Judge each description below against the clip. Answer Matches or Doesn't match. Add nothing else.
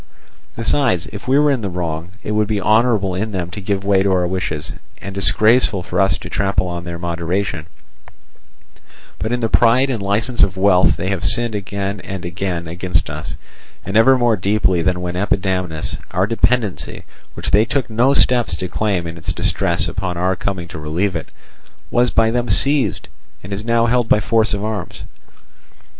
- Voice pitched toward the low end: Matches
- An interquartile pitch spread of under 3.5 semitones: Doesn't match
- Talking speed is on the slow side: Doesn't match